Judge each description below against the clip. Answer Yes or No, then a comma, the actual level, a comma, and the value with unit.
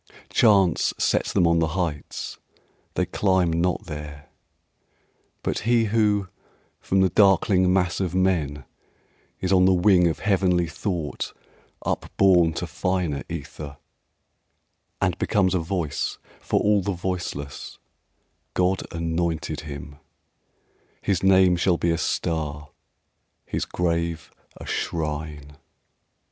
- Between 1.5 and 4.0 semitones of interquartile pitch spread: Yes, average, 2.9 semitones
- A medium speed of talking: No, slow, 115 wpm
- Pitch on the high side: No, very low, 90 Hz